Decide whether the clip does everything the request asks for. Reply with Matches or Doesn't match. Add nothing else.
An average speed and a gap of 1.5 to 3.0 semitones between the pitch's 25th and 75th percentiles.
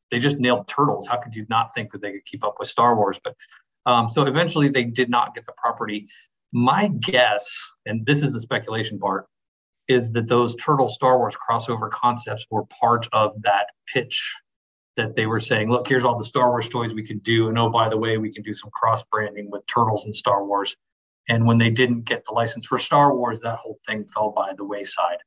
Doesn't match